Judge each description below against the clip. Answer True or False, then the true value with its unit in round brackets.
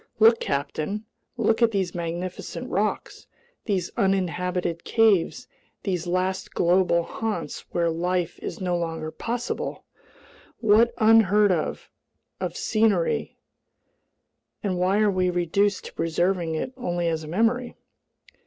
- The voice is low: False (185 Hz)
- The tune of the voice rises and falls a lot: False (3.7 semitones)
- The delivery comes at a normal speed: False (115 wpm)